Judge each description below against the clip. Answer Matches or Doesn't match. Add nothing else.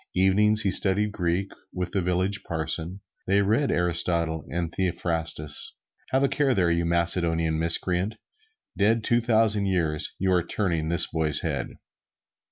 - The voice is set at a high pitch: Doesn't match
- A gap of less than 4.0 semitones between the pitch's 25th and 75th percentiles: Matches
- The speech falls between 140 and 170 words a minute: Matches